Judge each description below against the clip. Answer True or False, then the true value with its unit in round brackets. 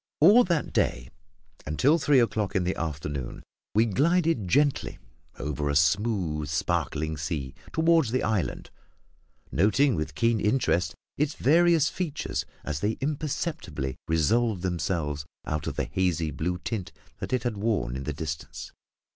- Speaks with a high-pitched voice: False (95 Hz)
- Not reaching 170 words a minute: True (145 wpm)